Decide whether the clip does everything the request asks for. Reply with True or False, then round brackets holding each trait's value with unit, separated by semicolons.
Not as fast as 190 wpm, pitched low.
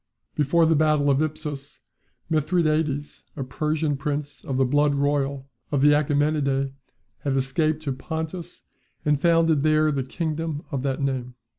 False (145 wpm; 145 Hz)